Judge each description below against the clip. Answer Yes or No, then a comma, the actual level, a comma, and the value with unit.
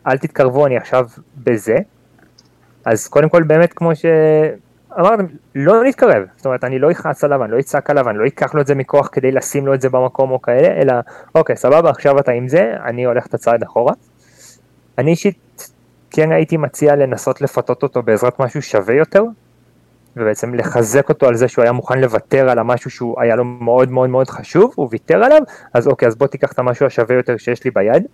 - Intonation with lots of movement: No, average, 3.0 semitones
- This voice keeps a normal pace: No, fast, 205 wpm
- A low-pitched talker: Yes, low, 130 Hz